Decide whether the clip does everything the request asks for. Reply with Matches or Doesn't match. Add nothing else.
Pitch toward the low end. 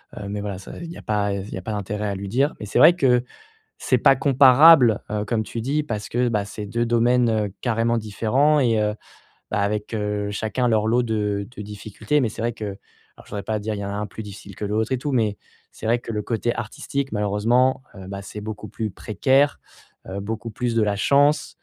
Matches